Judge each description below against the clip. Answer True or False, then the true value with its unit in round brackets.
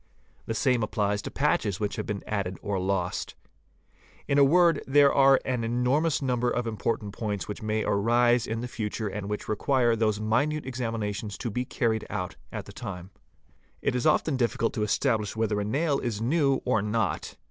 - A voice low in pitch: True (115 Hz)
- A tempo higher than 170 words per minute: True (190 wpm)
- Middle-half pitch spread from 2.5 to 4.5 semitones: True (3.5 semitones)